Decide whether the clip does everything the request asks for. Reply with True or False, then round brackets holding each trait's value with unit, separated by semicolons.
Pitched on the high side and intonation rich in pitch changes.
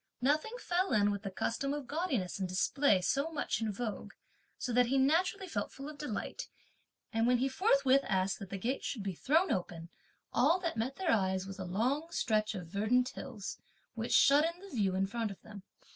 True (240 Hz; 6.4 semitones)